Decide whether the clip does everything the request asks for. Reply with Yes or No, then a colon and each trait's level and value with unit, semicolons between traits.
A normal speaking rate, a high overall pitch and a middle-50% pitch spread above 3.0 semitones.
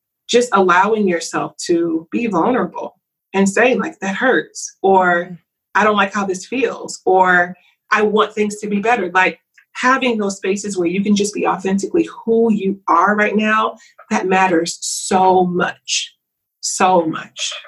Yes: average, 155 wpm; high, 200 Hz; average, 3.8 semitones